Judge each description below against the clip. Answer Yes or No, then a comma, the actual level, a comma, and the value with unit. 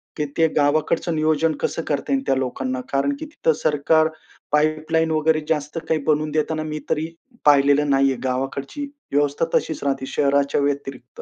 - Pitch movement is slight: Yes, narrow, 2.1 semitones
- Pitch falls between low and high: Yes, medium, 150 Hz